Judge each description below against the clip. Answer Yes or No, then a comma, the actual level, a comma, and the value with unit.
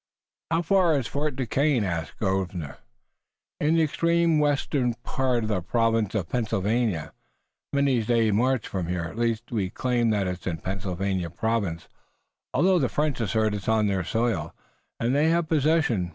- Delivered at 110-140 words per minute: No, average, 160 wpm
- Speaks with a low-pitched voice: Yes, low, 115 Hz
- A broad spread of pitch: Yes, wide, 6.4 semitones